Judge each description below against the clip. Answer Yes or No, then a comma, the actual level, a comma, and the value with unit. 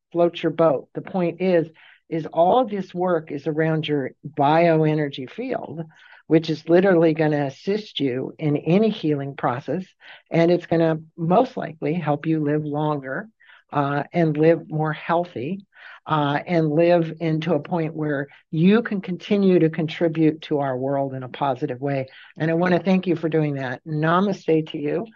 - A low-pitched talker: No, medium, 160 Hz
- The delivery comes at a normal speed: Yes, average, 175 wpm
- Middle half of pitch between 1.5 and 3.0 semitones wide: Yes, narrow, 2.6 semitones